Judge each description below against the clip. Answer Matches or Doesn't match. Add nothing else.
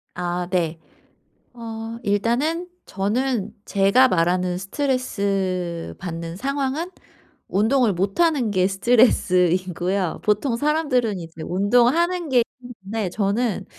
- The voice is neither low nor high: Doesn't match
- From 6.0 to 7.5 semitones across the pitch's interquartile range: Doesn't match